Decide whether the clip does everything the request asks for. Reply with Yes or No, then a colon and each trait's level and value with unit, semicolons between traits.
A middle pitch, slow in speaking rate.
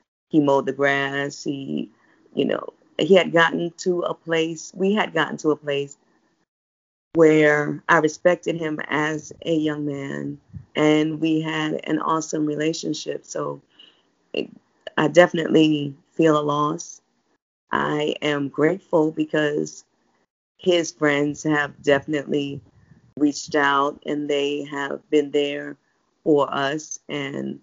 Yes: medium, 150 Hz; slow, 125 wpm